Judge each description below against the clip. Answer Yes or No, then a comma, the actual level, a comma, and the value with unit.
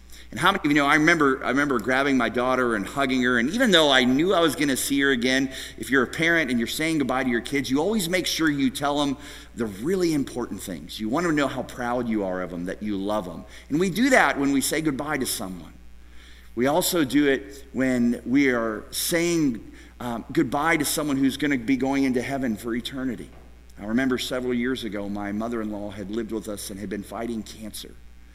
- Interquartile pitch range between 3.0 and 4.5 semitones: No, average, 5.2 semitones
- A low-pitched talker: Yes, low, 125 Hz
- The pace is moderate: No, fast, 240 wpm